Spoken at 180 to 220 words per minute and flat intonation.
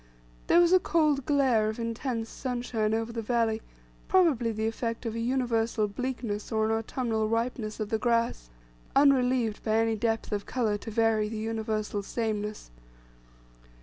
No: average, 155 wpm; narrow, 2.2 semitones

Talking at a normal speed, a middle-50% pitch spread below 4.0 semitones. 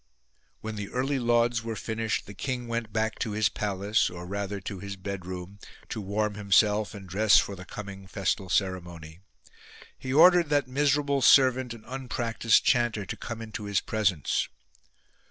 Yes: average, 160 wpm; average, 3.3 semitones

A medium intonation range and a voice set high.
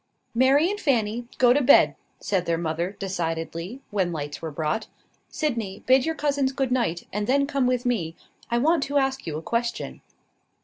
No: wide, 7.7 semitones; high, 235 Hz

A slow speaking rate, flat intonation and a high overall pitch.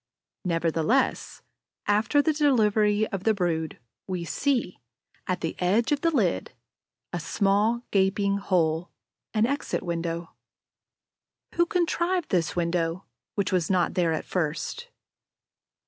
No: slow, 120 wpm; wide, 5.5 semitones; high, 195 Hz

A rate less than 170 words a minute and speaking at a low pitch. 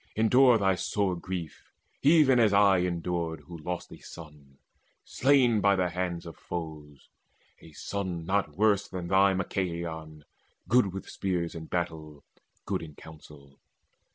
Yes: average, 140 wpm; very low, 90 Hz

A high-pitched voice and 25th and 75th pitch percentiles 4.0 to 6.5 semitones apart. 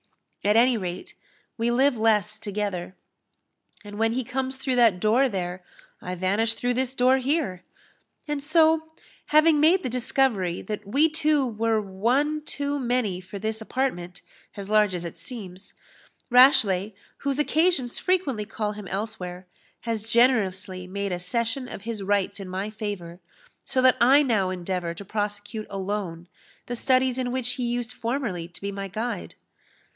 Yes: high, 220 Hz; average, 5.0 semitones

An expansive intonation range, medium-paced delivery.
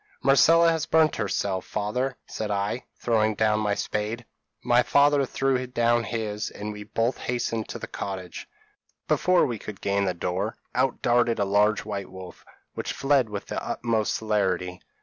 No: average, 3.4 semitones; average, 165 wpm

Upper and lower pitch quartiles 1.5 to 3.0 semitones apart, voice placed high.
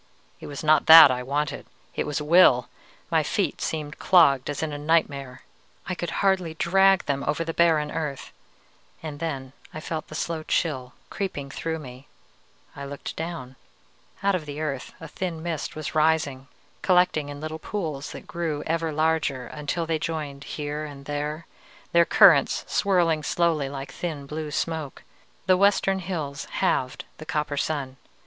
No: average, 2.7 semitones; medium, 155 Hz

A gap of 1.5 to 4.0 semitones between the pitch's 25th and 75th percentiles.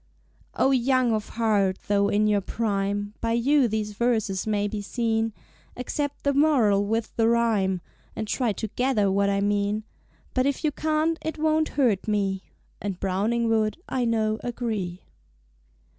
Yes: average, 3.4 semitones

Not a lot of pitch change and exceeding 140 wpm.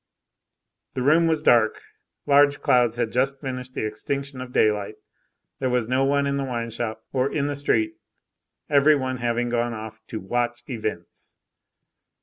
No: average, 3.1 semitones; average, 160 wpm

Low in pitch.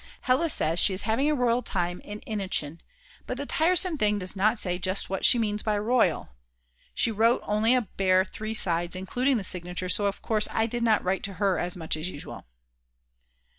No: high, 205 Hz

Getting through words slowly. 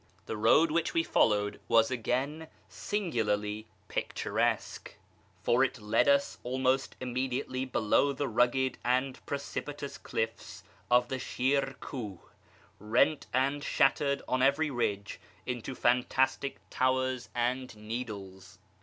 Yes: slow, 120 wpm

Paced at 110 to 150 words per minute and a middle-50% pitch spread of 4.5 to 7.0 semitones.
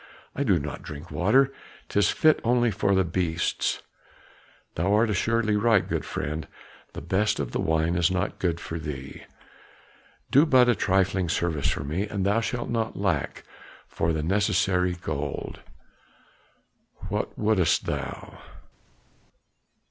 Yes: average, 140 wpm; average, 4.8 semitones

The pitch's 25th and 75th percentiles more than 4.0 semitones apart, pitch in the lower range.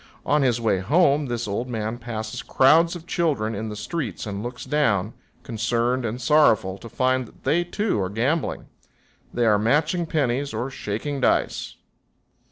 Yes: average, 5.2 semitones; low, 120 Hz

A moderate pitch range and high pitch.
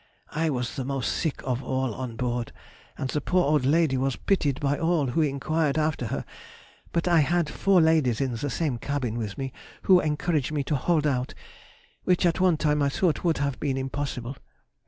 No: average, 3.5 semitones; medium, 145 Hz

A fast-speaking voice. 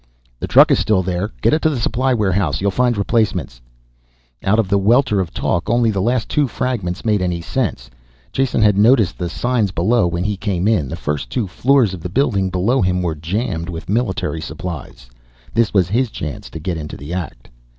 Yes: fast, 210 wpm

